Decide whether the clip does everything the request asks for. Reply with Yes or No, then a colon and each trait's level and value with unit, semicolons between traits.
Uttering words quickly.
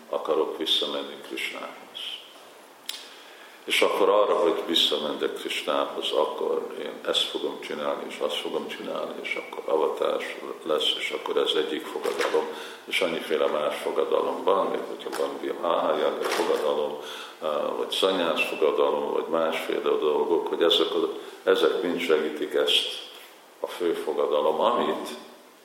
No: average, 130 wpm